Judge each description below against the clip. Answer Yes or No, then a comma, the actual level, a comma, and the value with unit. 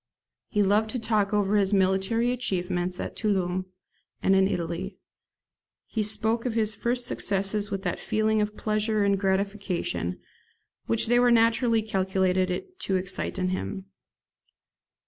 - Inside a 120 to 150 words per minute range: Yes, average, 140 wpm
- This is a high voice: Yes, high, 200 Hz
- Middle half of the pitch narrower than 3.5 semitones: Yes, narrow, 2.5 semitones